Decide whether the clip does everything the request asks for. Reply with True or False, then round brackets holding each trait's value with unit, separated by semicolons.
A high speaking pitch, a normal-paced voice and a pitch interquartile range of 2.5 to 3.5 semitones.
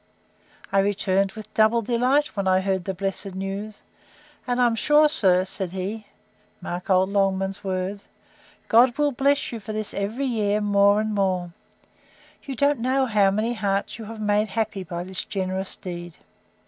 True (205 Hz; 170 wpm; 3.0 semitones)